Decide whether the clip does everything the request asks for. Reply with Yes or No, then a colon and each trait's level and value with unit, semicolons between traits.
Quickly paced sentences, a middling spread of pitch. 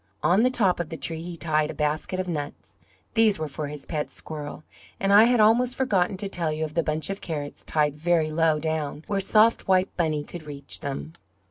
Yes: fast, 220 wpm; average, 4.3 semitones